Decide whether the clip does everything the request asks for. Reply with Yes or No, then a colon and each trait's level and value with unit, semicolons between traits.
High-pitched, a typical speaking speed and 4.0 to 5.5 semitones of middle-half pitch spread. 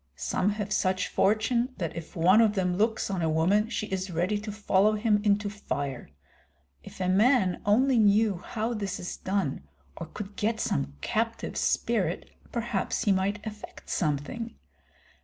No: high, 205 Hz; average, 160 wpm; average, 3.0 semitones